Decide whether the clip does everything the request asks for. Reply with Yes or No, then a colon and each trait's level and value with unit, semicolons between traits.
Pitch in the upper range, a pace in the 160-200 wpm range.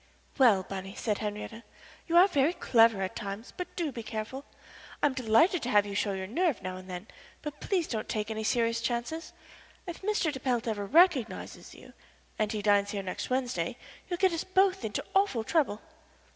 Yes: high, 235 Hz; average, 195 wpm